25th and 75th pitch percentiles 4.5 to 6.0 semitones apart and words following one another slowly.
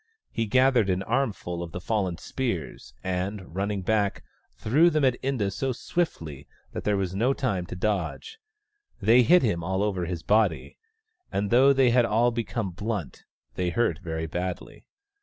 No: average, 5.1 semitones; average, 165 wpm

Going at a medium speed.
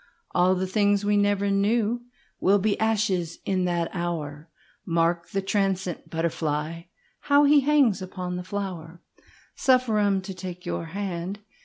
No: slow, 125 wpm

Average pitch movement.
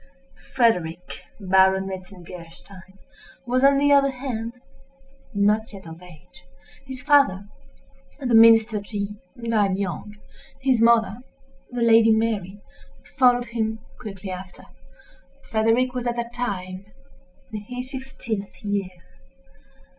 Yes: average, 4.1 semitones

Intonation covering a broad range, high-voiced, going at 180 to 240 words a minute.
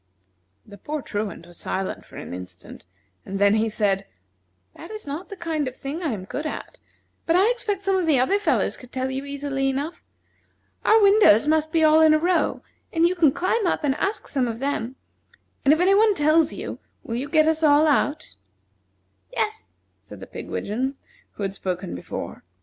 Yes: wide, 6.2 semitones; very high, 295 Hz; average, 195 wpm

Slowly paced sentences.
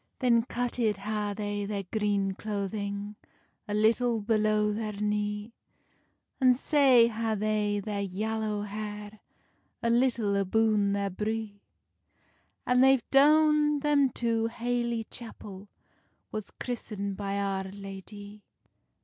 Yes: slow, 115 wpm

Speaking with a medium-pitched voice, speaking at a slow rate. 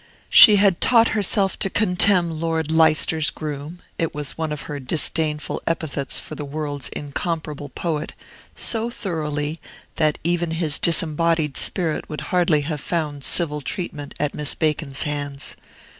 No: medium, 155 Hz; average, 145 wpm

